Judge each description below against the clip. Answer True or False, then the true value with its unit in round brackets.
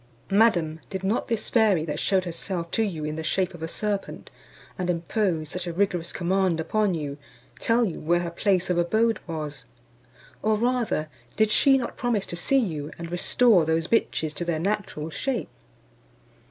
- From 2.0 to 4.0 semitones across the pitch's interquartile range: False (4.7 semitones)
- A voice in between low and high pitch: True (180 Hz)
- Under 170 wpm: False (180 wpm)